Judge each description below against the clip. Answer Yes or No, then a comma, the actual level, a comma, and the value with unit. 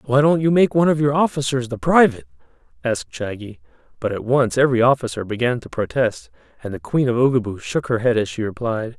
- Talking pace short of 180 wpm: No, fast, 205 wpm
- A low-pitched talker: Yes, low, 125 Hz